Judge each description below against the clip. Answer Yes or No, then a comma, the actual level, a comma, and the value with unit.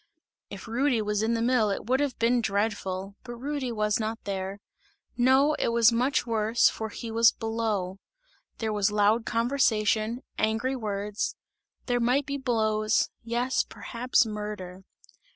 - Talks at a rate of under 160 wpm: Yes, average, 150 wpm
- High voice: Yes, high, 225 Hz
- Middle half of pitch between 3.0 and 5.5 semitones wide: No, narrow, 2.5 semitones